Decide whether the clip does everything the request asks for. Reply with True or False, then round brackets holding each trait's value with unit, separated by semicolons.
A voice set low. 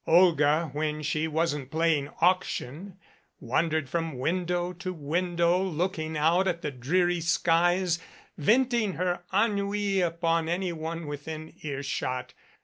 False (165 Hz)